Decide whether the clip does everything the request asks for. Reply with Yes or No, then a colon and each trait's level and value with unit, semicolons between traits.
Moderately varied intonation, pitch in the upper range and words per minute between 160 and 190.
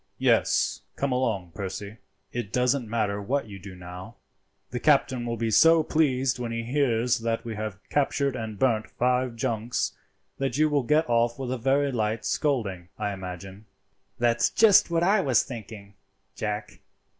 No: average, 4.0 semitones; low, 115 Hz; average, 165 wpm